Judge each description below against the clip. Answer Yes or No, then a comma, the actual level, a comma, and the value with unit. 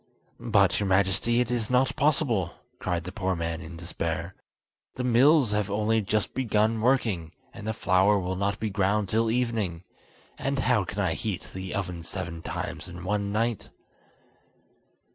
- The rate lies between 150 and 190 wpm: Yes, average, 160 wpm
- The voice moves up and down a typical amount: Yes, average, 3.8 semitones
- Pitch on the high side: No, low, 100 Hz